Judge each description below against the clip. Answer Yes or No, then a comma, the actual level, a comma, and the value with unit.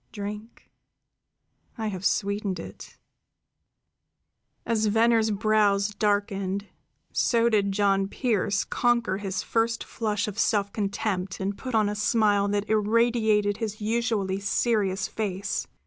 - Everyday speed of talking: No, slow, 115 wpm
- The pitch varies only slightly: Yes, narrow, 1.9 semitones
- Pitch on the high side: Yes, high, 210 Hz